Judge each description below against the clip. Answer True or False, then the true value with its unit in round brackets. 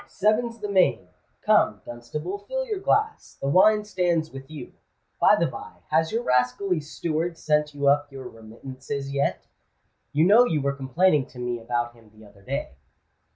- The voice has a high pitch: False (145 Hz)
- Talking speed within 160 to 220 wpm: True (170 wpm)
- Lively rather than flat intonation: True (6.8 semitones)